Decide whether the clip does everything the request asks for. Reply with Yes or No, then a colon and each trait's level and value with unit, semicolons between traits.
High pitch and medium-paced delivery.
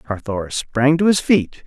No: low, 135 Hz; average, 180 wpm